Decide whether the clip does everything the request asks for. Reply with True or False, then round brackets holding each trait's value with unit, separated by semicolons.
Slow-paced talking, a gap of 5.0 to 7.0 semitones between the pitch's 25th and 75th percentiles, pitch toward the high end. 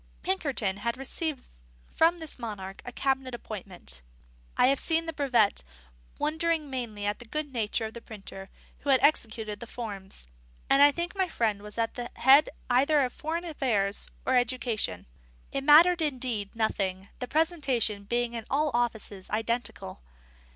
False (160 wpm; 5.4 semitones; 245 Hz)